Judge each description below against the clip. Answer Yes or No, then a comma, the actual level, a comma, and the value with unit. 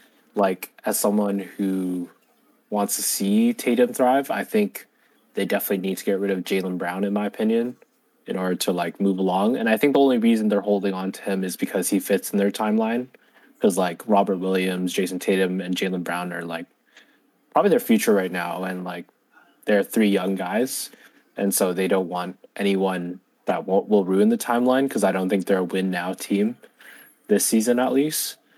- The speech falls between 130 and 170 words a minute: No, average, 195 wpm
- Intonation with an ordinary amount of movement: Yes, average, 3.1 semitones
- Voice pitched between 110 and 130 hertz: No, low, 100 Hz